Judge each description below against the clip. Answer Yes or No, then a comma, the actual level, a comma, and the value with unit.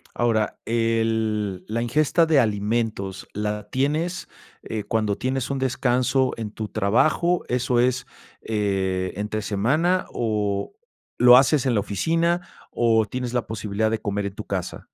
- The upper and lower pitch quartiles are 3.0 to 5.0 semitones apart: Yes, average, 3.6 semitones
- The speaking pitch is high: No, low, 115 Hz